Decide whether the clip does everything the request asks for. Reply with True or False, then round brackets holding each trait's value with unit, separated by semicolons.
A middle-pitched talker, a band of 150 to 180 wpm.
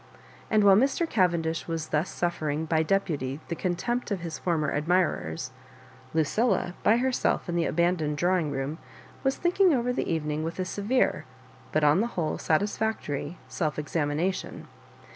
True (170 Hz; 165 wpm)